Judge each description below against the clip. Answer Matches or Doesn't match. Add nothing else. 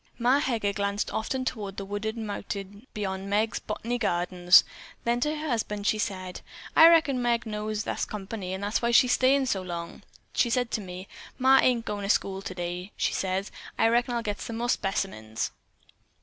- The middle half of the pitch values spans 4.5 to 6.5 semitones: Doesn't match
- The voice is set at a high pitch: Matches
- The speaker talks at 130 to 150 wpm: Doesn't match